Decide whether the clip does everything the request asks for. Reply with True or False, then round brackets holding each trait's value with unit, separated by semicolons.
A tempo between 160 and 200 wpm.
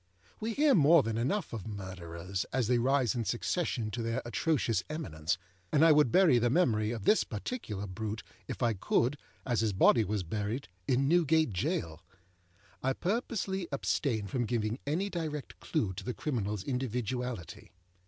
True (165 wpm)